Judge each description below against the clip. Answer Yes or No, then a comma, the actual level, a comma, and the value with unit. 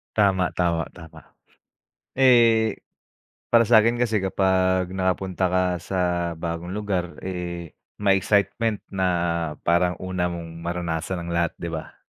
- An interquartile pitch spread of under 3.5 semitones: Yes, average, 2.8 semitones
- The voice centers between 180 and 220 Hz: No, very low, 95 Hz